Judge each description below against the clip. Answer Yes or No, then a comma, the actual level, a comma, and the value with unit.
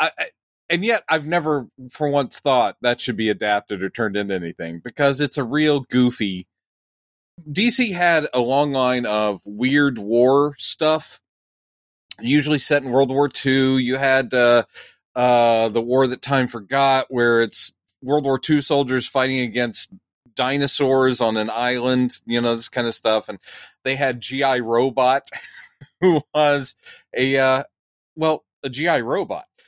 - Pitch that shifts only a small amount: No, average, 3.4 semitones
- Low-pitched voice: Yes, low, 130 Hz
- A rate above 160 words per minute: No, average, 155 wpm